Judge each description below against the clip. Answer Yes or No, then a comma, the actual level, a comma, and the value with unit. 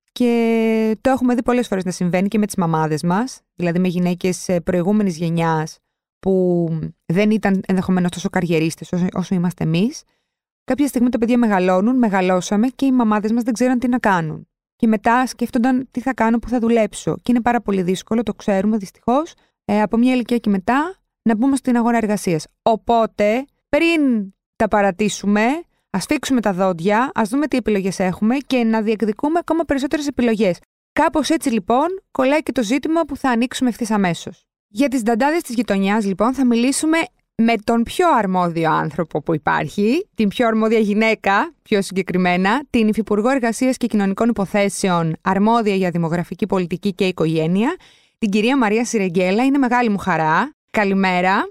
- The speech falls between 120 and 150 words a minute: No, average, 165 wpm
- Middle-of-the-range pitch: No, high, 220 Hz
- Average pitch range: Yes, average, 4.7 semitones